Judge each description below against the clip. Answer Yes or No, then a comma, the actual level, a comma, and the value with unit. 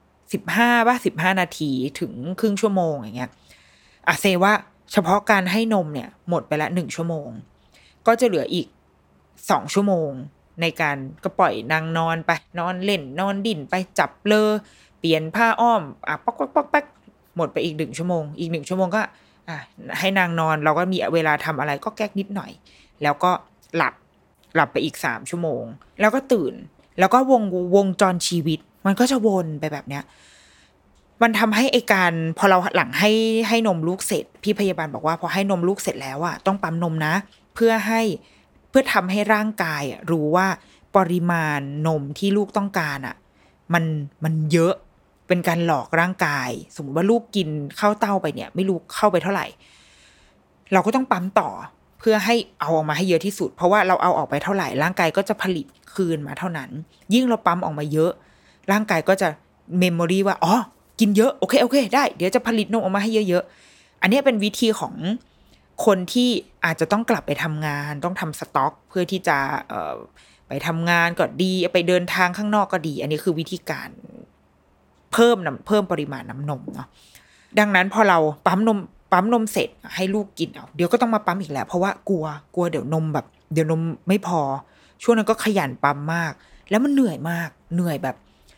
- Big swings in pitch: No, average, 4.8 semitones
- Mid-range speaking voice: Yes, medium, 180 Hz